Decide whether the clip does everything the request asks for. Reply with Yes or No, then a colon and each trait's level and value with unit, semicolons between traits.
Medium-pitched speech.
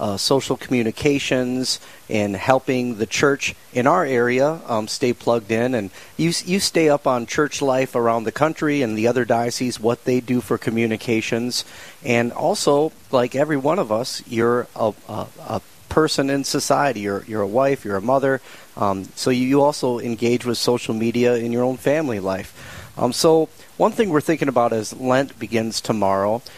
No: low, 125 Hz